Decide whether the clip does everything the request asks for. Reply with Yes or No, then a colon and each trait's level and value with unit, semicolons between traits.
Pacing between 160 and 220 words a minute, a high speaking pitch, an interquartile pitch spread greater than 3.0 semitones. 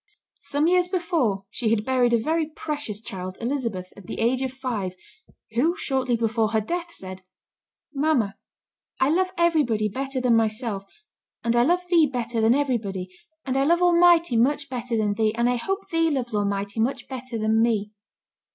Yes: average, 175 wpm; high, 245 Hz; average, 5.3 semitones